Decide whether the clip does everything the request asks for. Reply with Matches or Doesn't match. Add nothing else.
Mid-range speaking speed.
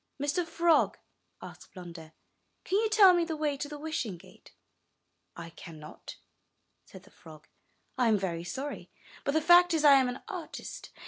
Matches